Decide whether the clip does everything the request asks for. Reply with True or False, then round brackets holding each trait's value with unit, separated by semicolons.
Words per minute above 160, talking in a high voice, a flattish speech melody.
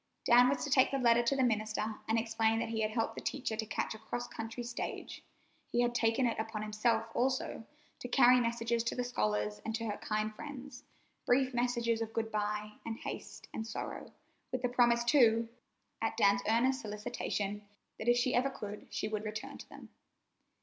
True (195 wpm; 230 Hz; 2.2 semitones)